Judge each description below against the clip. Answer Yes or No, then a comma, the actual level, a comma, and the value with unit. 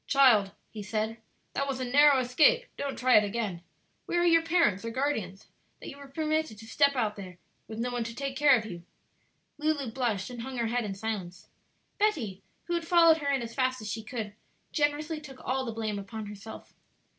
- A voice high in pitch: Yes, high, 245 Hz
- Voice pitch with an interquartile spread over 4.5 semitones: Yes, average, 5.0 semitones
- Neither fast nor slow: No, fast, 210 wpm